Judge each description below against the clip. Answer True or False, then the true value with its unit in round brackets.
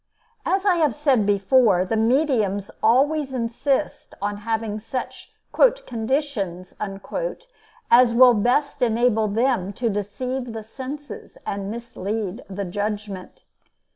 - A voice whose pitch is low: False (230 Hz)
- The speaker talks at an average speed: False (110 wpm)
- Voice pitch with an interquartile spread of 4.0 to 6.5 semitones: True (4.3 semitones)